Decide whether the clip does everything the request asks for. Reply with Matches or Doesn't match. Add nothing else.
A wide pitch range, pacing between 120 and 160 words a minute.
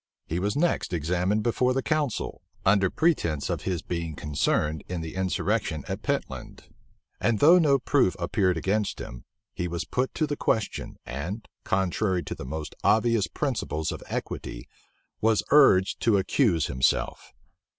Matches